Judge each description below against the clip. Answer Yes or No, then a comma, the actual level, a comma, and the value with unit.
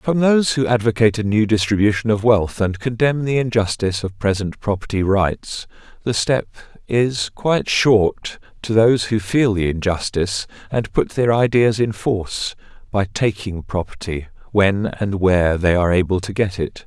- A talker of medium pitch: No, low, 105 Hz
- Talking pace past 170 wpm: No, average, 165 wpm